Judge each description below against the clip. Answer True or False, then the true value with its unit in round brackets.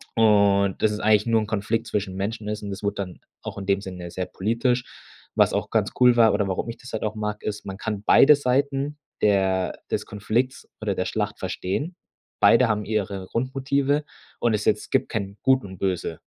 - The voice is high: False (105 Hz)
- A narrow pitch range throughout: False (3.1 semitones)